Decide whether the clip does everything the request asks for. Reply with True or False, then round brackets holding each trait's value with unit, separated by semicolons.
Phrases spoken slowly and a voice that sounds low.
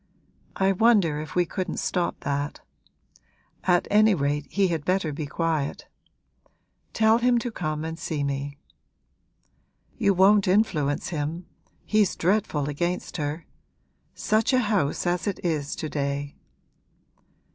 False (130 wpm; 170 Hz)